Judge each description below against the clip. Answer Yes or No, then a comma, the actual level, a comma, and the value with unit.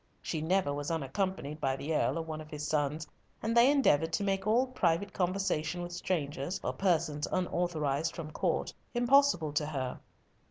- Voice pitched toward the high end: No, medium, 165 Hz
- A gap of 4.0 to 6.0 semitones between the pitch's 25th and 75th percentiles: Yes, average, 4.4 semitones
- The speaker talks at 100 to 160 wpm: No, average, 170 wpm